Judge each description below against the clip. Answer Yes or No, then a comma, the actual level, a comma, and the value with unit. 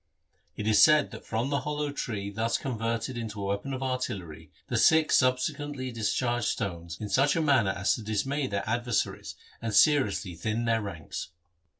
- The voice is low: Yes, low, 115 Hz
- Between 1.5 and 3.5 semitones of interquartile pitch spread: No, average, 4.8 semitones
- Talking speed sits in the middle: Yes, average, 175 wpm